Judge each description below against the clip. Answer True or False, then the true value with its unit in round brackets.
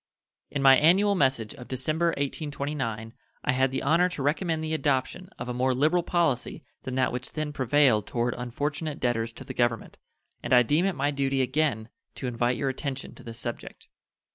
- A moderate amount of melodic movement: True (3.7 semitones)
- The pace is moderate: True (190 wpm)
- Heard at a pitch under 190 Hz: True (135 Hz)